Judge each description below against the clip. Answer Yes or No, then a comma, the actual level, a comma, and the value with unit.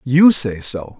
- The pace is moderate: Yes, average, 180 wpm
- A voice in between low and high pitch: No, low, 130 Hz